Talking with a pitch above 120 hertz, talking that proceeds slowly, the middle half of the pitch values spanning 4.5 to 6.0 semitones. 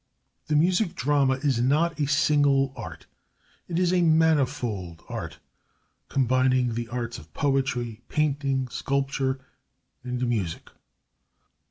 No: low, 135 Hz; slow, 115 wpm; average, 3.2 semitones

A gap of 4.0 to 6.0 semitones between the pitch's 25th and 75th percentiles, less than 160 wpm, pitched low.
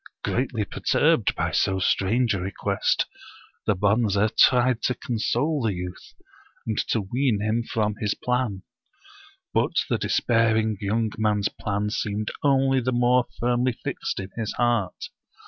No: average, 3.0 semitones; average, 145 wpm; low, 110 Hz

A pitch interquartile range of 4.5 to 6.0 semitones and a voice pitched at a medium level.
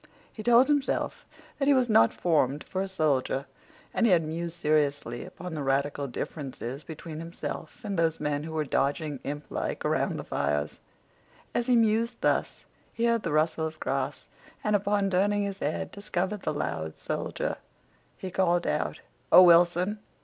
Yes: wide, 5.6 semitones; medium, 165 Hz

